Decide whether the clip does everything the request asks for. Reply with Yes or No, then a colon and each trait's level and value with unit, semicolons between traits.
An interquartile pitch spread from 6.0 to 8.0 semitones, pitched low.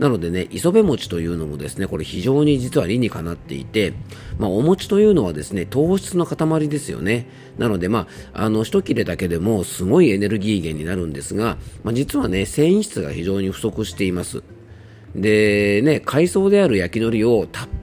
Yes: wide, 6.9 semitones; low, 110 Hz